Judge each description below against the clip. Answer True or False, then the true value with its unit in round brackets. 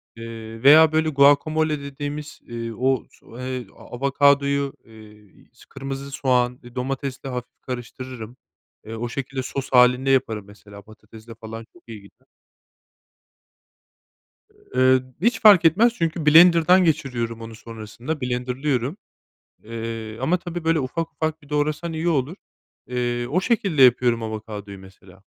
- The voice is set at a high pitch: False (130 Hz)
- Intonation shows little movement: False (4.7 semitones)